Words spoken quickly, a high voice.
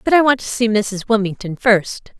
Yes: fast, 220 wpm; high, 220 Hz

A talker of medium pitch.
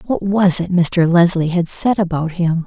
Yes: medium, 175 Hz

